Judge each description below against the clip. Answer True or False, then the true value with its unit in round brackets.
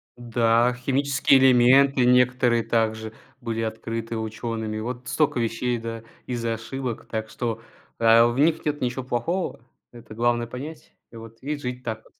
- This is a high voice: False (120 Hz)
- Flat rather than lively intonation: True (2.0 semitones)